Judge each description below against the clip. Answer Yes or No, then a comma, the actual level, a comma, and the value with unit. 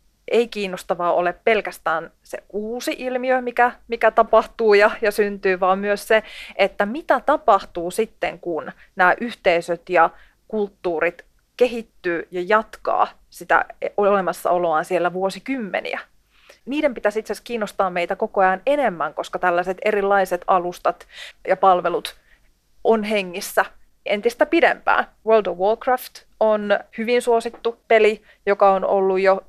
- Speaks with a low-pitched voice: No, high, 205 Hz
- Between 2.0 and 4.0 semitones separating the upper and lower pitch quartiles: Yes, average, 3.4 semitones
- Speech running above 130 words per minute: No, average, 125 wpm